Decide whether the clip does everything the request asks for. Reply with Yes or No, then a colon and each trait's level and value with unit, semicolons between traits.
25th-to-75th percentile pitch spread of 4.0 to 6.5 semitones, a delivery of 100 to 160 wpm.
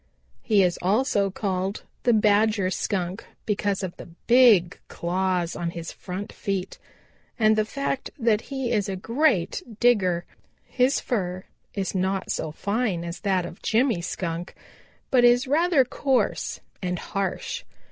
Yes: average, 4.7 semitones; average, 140 wpm